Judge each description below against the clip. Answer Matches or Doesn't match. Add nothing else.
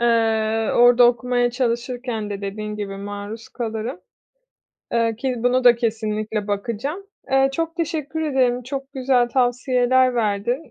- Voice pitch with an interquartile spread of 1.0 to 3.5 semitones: Matches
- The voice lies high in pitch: Matches